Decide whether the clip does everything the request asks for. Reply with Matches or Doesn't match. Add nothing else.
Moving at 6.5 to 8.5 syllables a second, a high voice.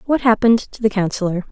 Matches